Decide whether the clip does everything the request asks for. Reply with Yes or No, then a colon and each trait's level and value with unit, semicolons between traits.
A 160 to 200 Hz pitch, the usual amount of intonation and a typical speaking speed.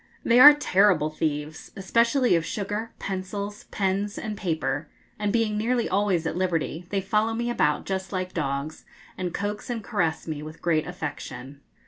Yes: high, 190 Hz; average, 4.8 semitones; average, 160 wpm